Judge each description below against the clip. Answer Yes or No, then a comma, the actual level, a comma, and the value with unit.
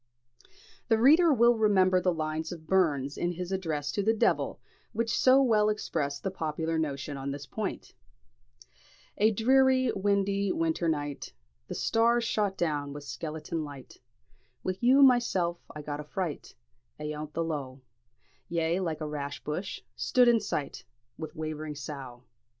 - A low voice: No, medium, 170 Hz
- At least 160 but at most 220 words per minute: No, average, 150 wpm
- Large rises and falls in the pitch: Yes, wide, 6.0 semitones